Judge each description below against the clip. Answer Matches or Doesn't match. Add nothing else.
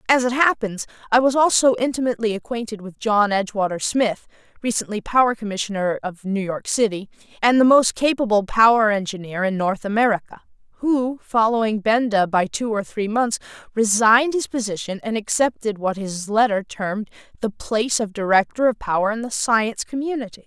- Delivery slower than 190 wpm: Matches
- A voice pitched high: Matches